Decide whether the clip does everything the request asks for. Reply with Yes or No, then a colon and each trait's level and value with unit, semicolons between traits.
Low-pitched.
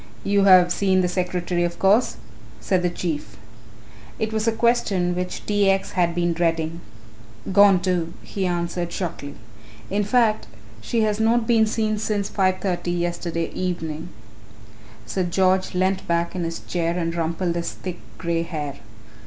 No: medium, 180 Hz